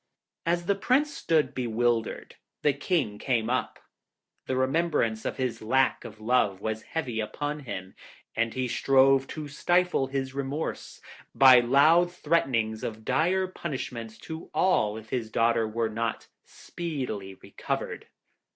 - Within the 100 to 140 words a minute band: Yes, slow, 135 wpm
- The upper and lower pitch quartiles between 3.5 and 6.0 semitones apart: Yes, wide, 5.6 semitones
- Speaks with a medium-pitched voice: No, low, 130 Hz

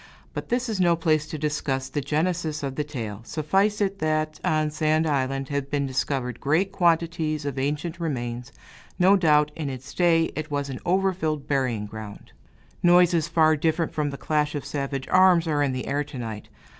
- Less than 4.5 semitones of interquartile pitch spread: Yes, average, 3.4 semitones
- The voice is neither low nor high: Yes, medium, 150 Hz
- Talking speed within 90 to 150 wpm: No, average, 190 wpm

